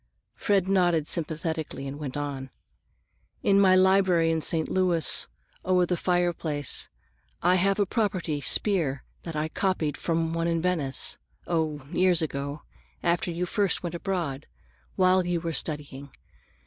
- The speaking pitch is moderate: Yes, medium, 170 Hz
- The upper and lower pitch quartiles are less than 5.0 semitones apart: Yes, average, 3.3 semitones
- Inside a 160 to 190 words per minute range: No, slow, 135 wpm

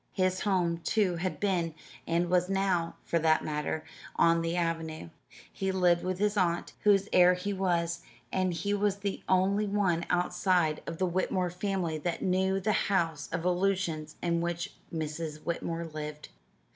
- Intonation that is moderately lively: No, narrow, 2.3 semitones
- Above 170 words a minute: No, average, 160 wpm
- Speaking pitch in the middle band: Yes, medium, 175 Hz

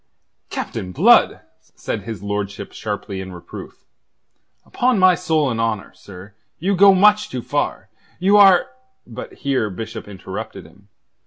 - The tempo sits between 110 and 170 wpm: Yes, average, 140 wpm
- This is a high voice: No, low, 115 Hz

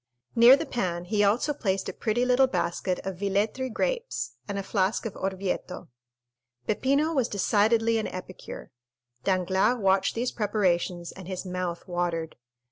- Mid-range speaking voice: No, high, 200 Hz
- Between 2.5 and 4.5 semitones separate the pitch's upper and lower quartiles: Yes, average, 4.2 semitones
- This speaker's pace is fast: No, average, 145 wpm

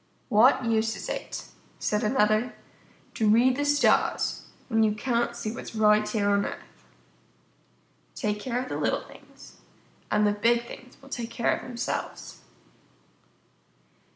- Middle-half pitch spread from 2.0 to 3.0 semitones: Yes, narrow, 2.5 semitones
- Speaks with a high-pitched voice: Yes, high, 230 Hz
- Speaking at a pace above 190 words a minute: No, average, 150 wpm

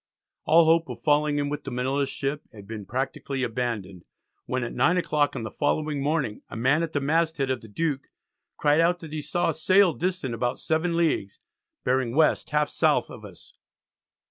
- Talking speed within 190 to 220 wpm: Yes, average, 195 wpm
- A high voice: No, medium, 145 Hz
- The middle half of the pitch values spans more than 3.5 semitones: Yes, average, 4.2 semitones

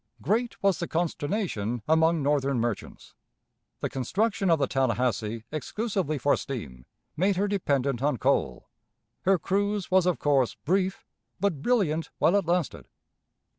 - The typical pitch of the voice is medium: Yes, medium, 160 Hz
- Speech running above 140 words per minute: No, slow, 135 wpm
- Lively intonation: Yes, wide, 6.4 semitones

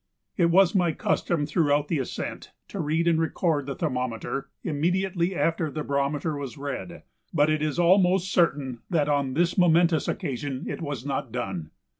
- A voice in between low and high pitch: Yes, medium, 155 Hz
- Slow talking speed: No, average, 165 wpm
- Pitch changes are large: No, average, 3.5 semitones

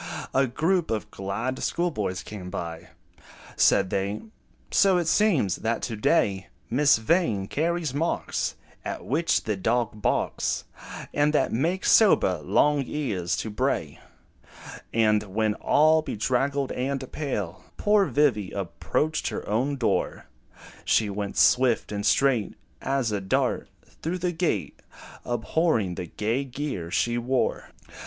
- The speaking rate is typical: No, slow, 130 wpm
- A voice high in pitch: No, low, 120 Hz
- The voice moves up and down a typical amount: No, wide, 6.5 semitones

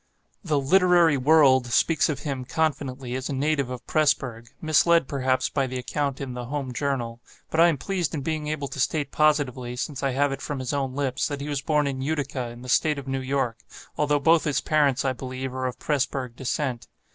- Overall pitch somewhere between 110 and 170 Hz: Yes, medium, 140 Hz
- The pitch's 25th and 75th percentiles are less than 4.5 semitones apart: Yes, average, 2.7 semitones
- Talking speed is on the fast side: Yes, fast, 215 wpm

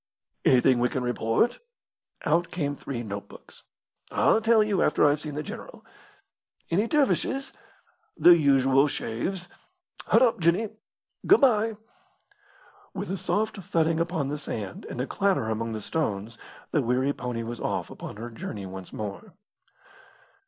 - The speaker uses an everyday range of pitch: No, wide, 8.2 semitones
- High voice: No, medium, 145 Hz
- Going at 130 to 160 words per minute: Yes, average, 145 wpm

